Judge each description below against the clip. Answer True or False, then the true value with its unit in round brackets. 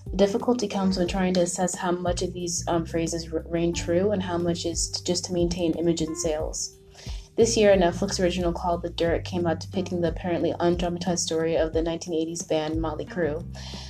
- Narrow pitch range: True (1.6 semitones)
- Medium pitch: True (170 Hz)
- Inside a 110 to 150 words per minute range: False (205 wpm)